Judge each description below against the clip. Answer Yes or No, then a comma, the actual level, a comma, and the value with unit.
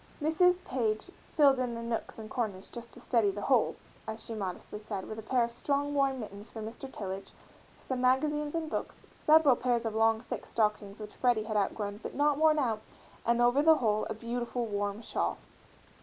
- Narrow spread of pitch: No, average, 4.0 semitones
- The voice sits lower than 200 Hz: No, high, 235 Hz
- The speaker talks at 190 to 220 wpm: Yes, average, 200 wpm